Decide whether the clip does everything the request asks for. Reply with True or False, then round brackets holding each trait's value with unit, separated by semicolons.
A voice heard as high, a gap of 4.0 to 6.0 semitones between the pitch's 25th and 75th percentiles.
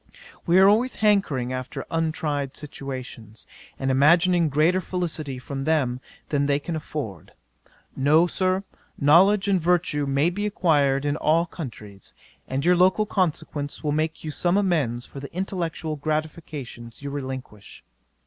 False (155 Hz; 4.3 semitones)